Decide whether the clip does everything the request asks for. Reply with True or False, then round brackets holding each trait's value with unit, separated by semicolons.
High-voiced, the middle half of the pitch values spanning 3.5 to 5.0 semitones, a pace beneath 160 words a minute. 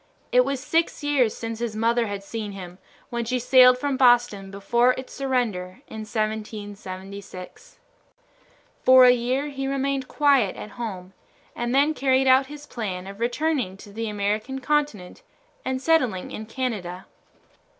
True (240 Hz; 4.5 semitones; 150 wpm)